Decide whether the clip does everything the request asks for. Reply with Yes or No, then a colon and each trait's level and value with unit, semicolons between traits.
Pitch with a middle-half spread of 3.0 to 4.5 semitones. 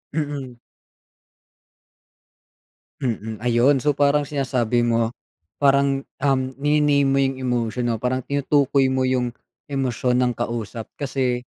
No: narrow, 2.6 semitones